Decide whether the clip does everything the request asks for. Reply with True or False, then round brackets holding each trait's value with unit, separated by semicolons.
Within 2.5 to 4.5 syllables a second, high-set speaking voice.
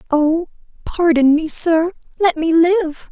True (3.6 syllables/s; 330 Hz)